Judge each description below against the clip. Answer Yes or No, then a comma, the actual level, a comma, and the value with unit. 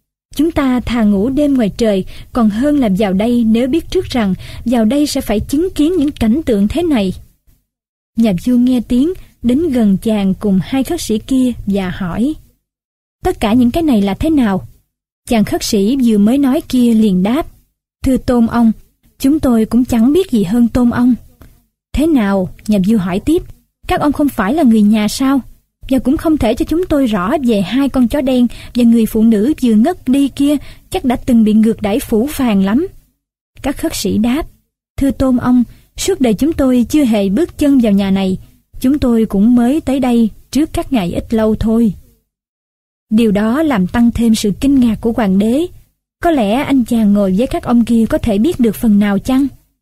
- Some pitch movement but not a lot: Yes, average, 4.2 semitones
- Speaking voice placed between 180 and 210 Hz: No, high, 245 Hz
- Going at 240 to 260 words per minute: No, average, 205 wpm